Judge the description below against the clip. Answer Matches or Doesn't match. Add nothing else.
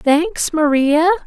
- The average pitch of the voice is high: Matches